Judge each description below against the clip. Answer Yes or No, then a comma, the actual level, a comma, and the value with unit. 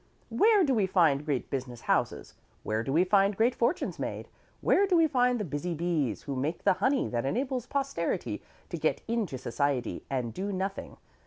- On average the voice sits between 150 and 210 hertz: Yes, medium, 185 Hz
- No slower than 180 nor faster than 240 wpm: Yes, average, 185 wpm